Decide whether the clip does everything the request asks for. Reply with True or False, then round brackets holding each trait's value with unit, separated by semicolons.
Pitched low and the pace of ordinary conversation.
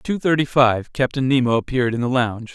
False (130 Hz; 235 wpm)